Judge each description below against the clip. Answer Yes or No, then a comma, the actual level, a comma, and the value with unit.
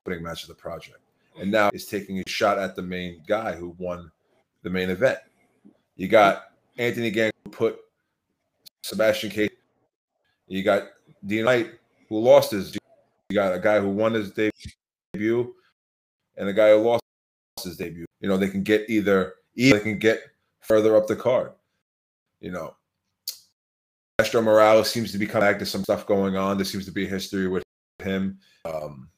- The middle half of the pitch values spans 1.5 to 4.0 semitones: Yes, average, 3.0 semitones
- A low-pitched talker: Yes, low, 100 Hz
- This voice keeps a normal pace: Yes, average, 175 wpm